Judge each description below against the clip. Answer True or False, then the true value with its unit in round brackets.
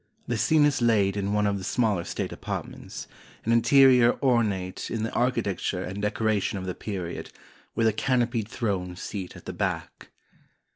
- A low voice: True (110 Hz)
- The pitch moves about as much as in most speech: True (3.4 semitones)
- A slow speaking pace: False (165 wpm)